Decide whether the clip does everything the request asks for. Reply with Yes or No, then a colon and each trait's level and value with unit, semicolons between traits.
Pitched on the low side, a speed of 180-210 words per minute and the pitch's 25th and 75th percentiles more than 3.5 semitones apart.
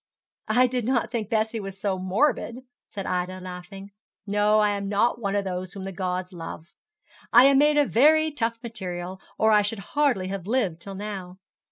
No: high, 205 Hz; average, 190 wpm; average, 3.9 semitones